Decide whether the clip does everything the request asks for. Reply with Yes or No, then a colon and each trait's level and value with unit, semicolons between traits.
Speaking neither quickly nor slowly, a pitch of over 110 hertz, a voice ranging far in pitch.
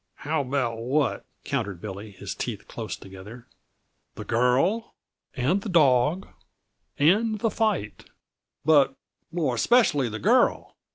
No: slow, 120 wpm; low, 135 Hz; wide, 7.1 semitones